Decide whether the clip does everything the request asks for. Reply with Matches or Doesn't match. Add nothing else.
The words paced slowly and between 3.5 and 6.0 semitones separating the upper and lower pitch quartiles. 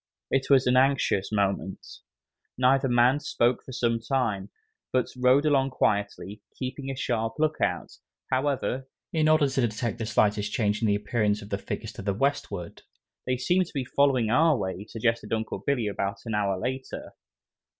Doesn't match